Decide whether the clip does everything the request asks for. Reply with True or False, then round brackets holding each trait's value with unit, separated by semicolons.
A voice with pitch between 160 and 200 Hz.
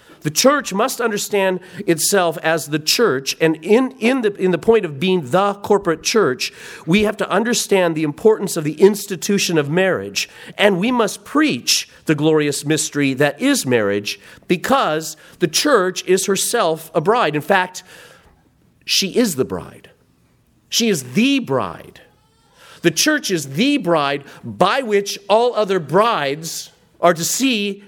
True (185 Hz)